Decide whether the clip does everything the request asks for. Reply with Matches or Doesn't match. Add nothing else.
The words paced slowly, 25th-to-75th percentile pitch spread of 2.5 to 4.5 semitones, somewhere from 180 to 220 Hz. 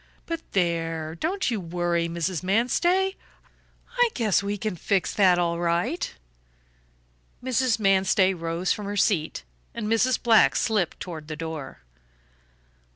Doesn't match